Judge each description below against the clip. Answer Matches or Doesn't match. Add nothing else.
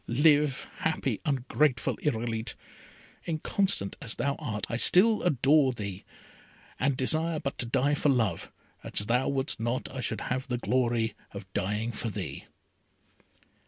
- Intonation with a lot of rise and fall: Doesn't match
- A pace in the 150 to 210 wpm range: Doesn't match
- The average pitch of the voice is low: Matches